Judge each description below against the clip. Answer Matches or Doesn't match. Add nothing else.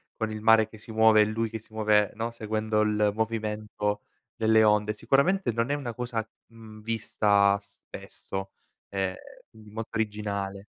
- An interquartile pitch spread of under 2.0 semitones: Matches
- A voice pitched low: Matches